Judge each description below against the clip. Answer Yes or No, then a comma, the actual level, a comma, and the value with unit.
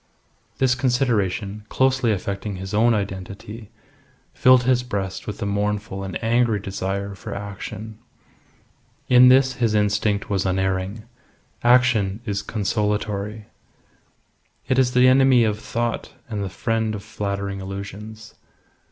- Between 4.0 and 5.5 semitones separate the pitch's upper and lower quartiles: No, average, 3.2 semitones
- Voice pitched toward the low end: Yes, low, 105 Hz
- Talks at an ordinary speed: No, slow, 125 wpm